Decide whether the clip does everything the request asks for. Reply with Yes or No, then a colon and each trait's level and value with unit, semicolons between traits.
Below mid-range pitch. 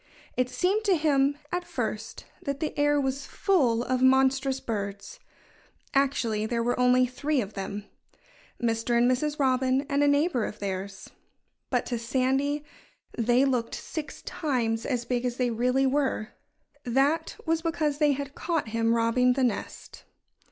No: very high, 260 Hz